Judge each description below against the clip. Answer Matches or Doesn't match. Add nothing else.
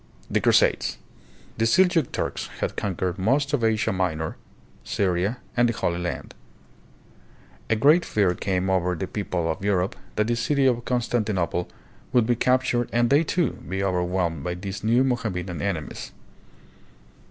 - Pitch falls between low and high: Doesn't match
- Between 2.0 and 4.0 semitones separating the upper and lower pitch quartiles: Doesn't match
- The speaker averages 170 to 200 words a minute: Doesn't match